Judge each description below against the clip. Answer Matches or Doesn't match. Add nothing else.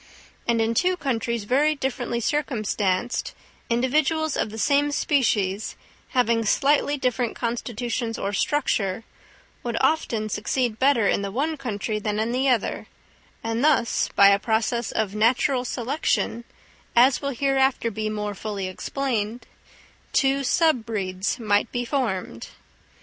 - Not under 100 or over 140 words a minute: Matches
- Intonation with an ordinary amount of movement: Matches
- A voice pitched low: Doesn't match